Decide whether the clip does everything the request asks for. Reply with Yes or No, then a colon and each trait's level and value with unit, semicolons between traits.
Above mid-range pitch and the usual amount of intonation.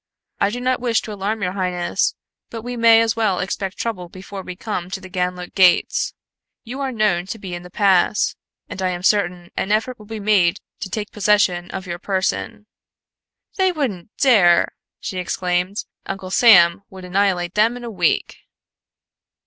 Yes: high, 195 Hz; average, 3.4 semitones